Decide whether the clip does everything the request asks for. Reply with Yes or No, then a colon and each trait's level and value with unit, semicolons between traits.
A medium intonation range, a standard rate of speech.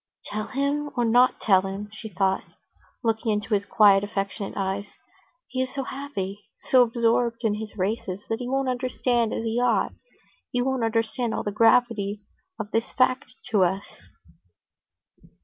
Yes: average, 3.5 semitones; average, 160 wpm